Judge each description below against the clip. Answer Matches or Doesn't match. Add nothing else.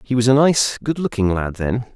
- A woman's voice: Doesn't match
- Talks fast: Matches